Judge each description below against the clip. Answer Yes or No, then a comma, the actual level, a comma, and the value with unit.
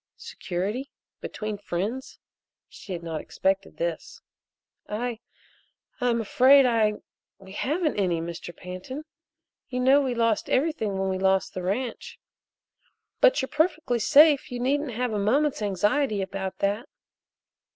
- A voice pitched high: Yes, high, 225 Hz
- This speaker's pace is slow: Yes, slow, 130 wpm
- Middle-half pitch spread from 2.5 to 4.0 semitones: No, wide, 5.6 semitones